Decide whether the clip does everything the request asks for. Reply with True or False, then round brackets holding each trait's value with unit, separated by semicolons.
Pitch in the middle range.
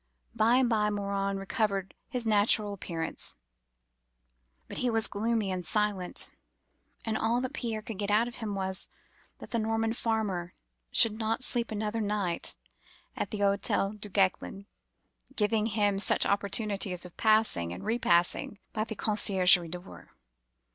False (210 Hz)